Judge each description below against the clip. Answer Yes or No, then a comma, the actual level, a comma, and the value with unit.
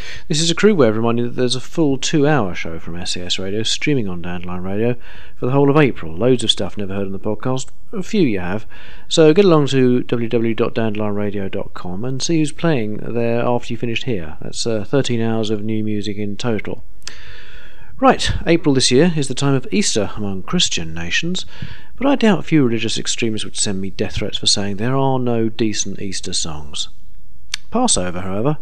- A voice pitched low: Yes, low, 115 Hz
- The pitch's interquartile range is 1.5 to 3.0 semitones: No, average, 5.2 semitones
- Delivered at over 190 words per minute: Yes, average, 200 wpm